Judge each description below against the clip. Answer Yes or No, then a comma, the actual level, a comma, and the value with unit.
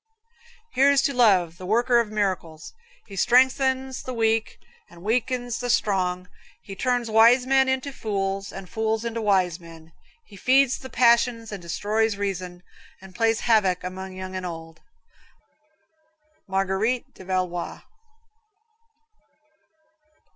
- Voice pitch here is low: No, high, 215 Hz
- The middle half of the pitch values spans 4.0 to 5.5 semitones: Yes, average, 4.6 semitones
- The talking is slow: Yes, slow, 125 wpm